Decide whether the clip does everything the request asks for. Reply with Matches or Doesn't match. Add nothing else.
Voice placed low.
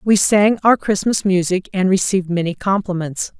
Doesn't match